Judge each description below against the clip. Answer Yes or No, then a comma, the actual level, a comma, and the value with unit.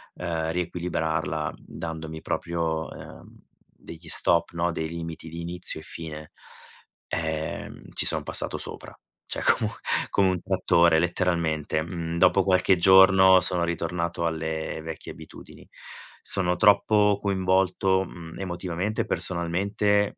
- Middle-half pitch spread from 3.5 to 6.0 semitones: No, narrow, 2.5 semitones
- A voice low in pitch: Yes, very low, 85 Hz